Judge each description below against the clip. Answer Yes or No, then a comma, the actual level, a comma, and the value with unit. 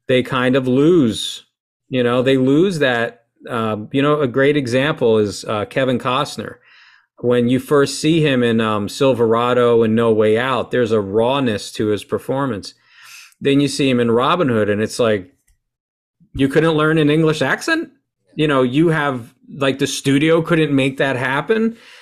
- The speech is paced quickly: No, average, 175 wpm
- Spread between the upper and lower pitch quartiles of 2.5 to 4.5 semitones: Yes, average, 4.0 semitones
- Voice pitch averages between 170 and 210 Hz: No, low, 135 Hz